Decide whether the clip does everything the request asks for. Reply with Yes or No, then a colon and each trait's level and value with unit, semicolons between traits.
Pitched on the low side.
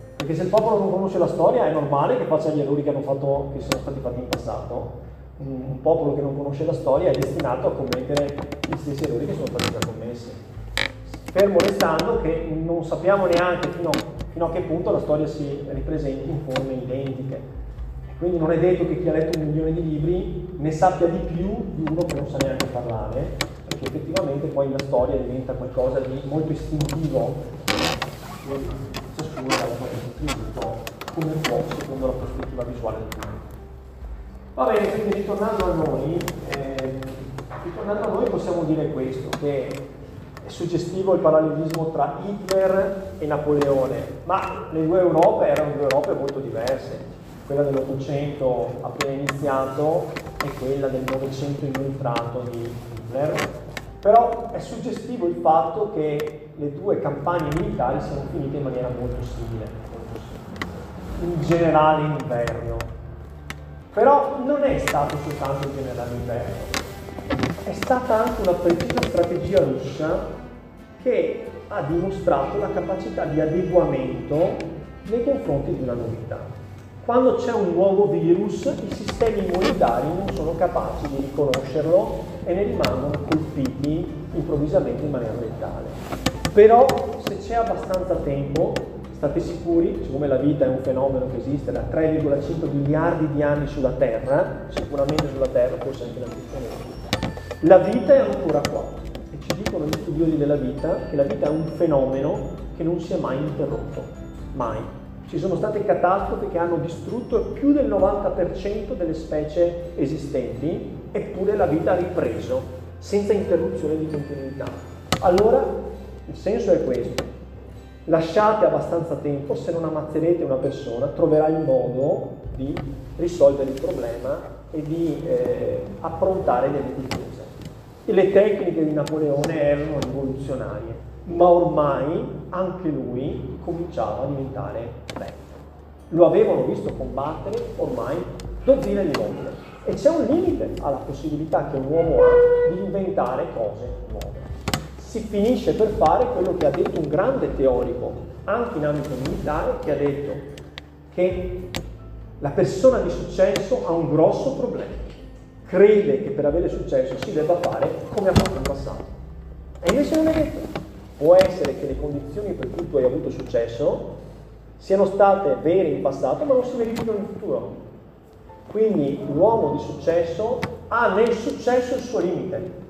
No: medium, 155 Hz